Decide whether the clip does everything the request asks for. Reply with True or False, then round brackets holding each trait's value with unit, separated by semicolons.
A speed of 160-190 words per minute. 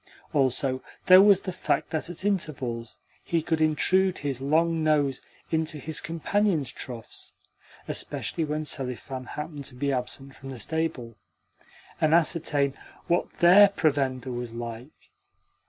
False (135 wpm)